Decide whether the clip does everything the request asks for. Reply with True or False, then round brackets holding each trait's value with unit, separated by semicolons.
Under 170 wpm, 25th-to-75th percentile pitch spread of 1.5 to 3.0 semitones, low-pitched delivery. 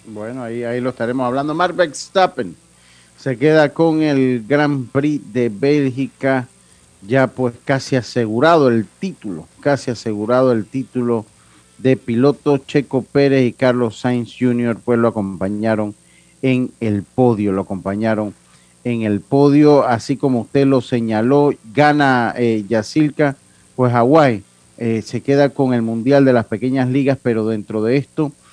False (145 wpm; 3.8 semitones; 125 Hz)